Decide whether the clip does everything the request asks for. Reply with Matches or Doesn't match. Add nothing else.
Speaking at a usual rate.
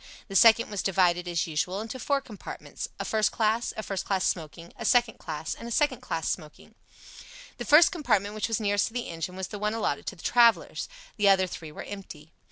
Doesn't match